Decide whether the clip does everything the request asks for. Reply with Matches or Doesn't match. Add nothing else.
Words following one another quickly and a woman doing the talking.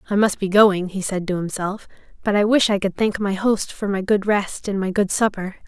Matches